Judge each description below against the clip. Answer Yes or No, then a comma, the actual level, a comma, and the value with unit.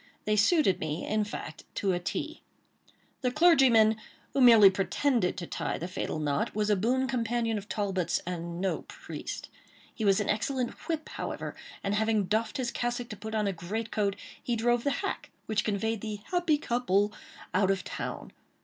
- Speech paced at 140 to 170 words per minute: No, average, 180 wpm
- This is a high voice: Yes, high, 215 Hz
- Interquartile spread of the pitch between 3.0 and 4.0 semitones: Yes, average, 3.7 semitones